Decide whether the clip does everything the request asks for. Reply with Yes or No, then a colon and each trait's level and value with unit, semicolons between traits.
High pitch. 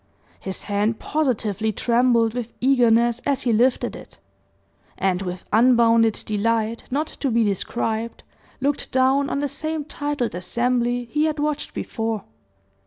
Yes: high, 235 Hz